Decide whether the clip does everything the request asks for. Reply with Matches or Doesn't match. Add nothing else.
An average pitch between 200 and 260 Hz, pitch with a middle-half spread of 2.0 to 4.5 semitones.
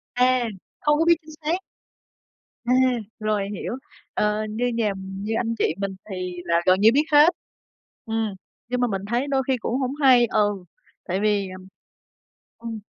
Matches